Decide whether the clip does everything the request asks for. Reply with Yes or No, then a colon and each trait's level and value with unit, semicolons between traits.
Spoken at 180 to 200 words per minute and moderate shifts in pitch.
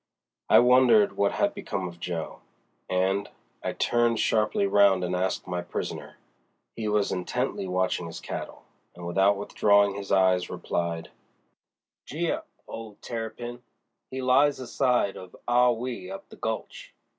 No: average, 140 wpm; average, 4.7 semitones